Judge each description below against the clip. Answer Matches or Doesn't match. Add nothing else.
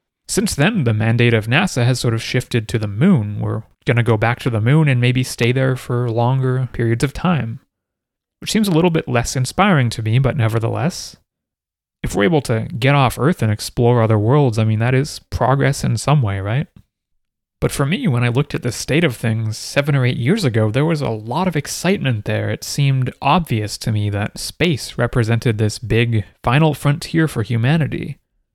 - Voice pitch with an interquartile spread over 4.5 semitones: Doesn't match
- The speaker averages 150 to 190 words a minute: Doesn't match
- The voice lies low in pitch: Matches